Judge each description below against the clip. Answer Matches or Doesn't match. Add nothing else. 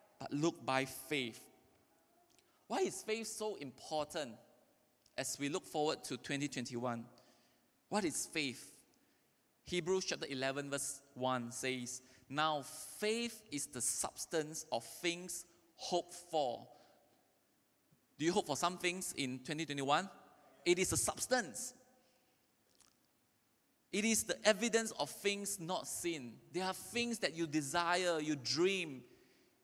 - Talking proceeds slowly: Matches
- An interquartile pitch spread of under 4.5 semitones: Doesn't match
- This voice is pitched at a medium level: Matches